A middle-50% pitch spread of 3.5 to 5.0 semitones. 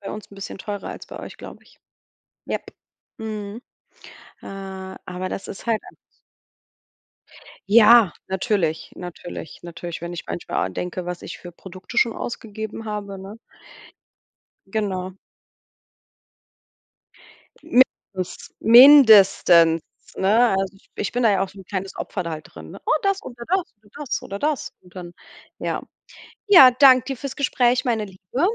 Yes: average, 4.4 semitones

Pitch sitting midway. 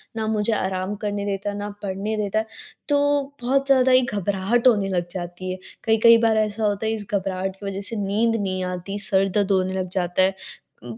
No: high, 205 Hz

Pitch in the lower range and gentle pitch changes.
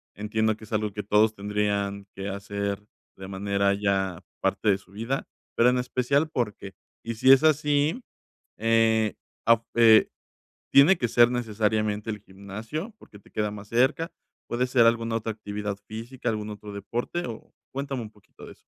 No: low, 110 Hz; average, 3.0 semitones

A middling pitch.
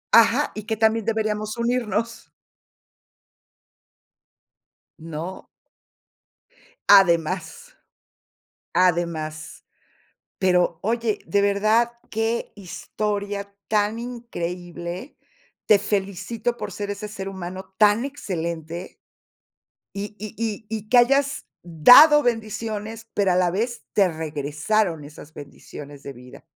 No: high, 205 Hz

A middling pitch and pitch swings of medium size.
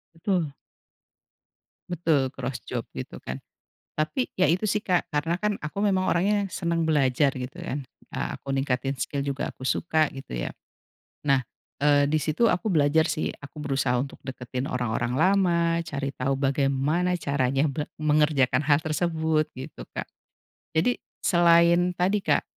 Yes: medium, 150 Hz; average, 4.1 semitones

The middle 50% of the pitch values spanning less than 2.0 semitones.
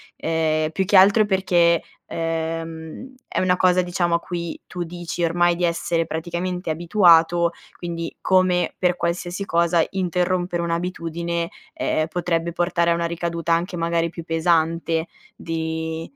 Yes: narrow, 1.3 semitones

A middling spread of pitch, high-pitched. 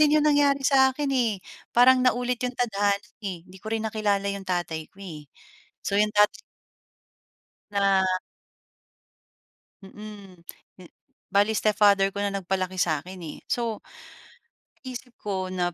Yes: average, 4.3 semitones; high, 205 Hz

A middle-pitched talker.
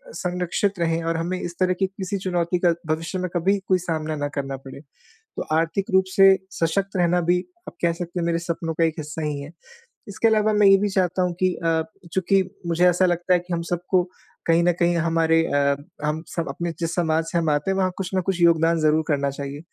Yes: medium, 170 Hz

